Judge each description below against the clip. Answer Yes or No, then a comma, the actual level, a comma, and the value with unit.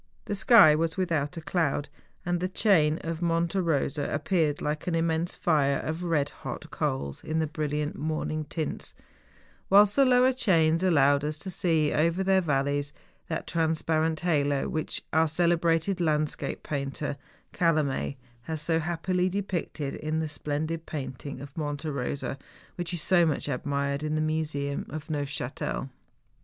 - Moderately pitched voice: Yes, medium, 155 Hz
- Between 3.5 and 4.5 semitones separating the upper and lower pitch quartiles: No, average, 2.7 semitones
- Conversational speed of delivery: Yes, average, 150 wpm